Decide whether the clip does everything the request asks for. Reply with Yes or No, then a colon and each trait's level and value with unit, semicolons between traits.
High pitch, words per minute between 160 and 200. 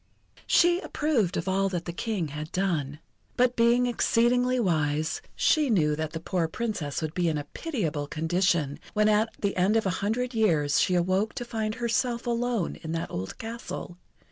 Yes: high, 195 Hz; average, 180 wpm